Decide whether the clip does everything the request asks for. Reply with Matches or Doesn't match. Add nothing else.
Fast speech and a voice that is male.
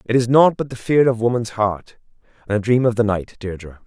Matches